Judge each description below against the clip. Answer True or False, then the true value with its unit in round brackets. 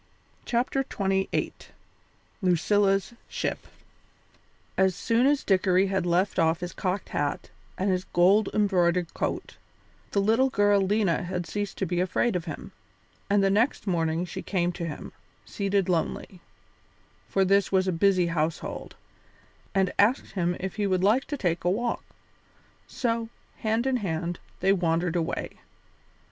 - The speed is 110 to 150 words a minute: True (145 wpm)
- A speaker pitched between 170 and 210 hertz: True (190 Hz)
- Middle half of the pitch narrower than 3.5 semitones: True (2.7 semitones)